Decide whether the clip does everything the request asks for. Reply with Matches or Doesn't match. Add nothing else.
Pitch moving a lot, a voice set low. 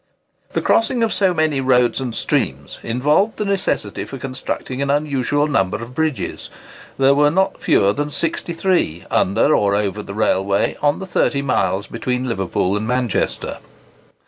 Matches